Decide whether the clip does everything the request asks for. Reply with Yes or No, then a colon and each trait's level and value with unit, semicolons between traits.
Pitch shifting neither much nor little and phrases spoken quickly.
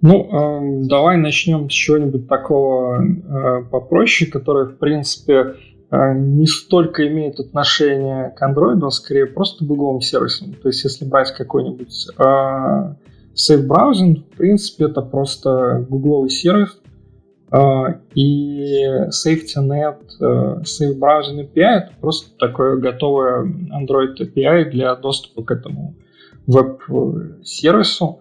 No: average, 3.0 semitones; average, 120 wpm